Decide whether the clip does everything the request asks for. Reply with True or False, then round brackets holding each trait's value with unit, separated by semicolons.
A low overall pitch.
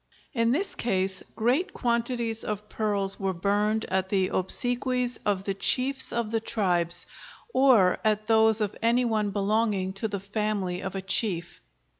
False (215 Hz)